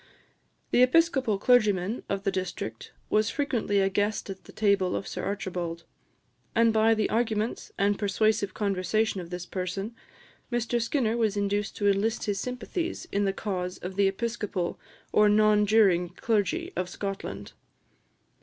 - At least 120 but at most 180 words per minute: Yes, average, 150 wpm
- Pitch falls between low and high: No, high, 205 Hz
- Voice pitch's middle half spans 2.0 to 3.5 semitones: Yes, narrow, 2.6 semitones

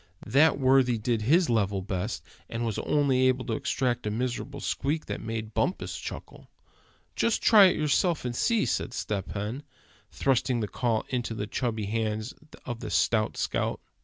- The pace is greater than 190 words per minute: No, average, 165 wpm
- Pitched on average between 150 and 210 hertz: No, low, 120 Hz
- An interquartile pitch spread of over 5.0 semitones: No, average, 4.0 semitones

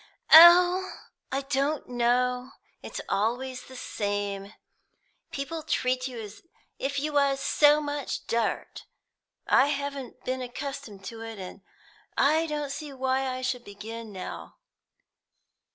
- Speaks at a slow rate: Yes, slow, 125 wpm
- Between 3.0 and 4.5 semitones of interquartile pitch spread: Yes, average, 3.6 semitones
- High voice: Yes, very high, 260 Hz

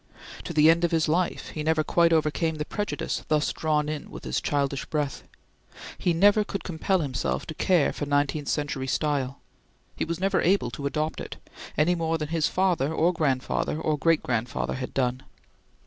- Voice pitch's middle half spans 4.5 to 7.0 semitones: No, average, 2.7 semitones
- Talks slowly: No, average, 185 wpm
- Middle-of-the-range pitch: Yes, medium, 155 Hz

